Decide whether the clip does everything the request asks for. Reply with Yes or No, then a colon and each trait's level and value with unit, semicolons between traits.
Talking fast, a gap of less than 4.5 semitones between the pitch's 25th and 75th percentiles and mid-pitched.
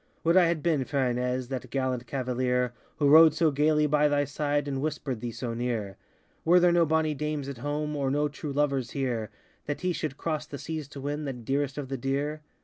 Yes: fast, 220 wpm; average, 2.8 semitones; medium, 145 Hz